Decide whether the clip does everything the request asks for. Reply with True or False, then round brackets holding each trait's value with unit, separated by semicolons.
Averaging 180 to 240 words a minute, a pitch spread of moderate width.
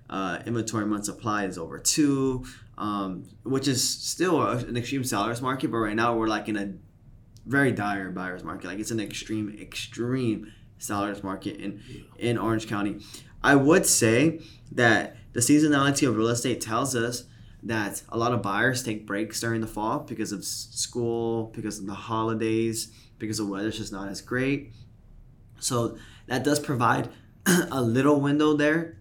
False (165 wpm; 3.0 semitones)